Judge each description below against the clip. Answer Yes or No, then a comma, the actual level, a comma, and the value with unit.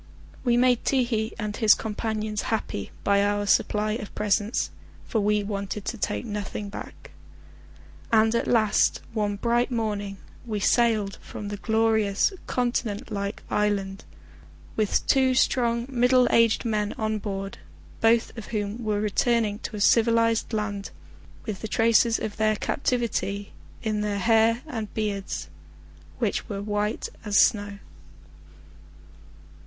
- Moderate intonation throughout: No, narrow, 2.0 semitones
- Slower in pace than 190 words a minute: Yes, average, 140 wpm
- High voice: Yes, high, 215 Hz